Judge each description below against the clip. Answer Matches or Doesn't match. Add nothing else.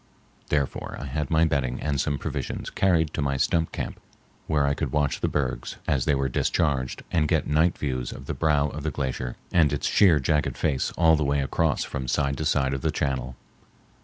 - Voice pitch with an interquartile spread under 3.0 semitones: Matches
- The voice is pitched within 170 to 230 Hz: Doesn't match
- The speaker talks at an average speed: Doesn't match